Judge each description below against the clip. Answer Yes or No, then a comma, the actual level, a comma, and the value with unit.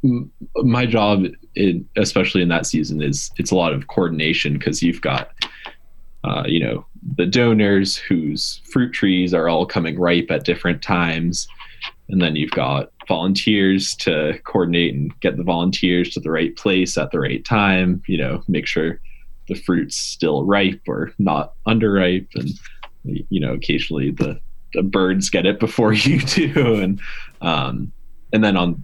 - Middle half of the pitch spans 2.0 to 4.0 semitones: Yes, average, 3.4 semitones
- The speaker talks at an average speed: Yes, average, 160 wpm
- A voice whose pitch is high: No, very low, 95 Hz